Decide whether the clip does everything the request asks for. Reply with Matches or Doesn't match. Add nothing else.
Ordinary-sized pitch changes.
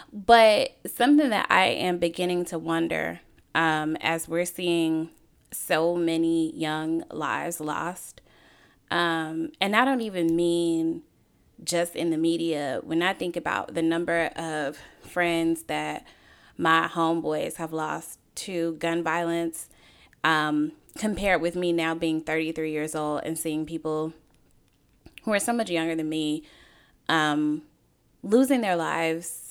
Doesn't match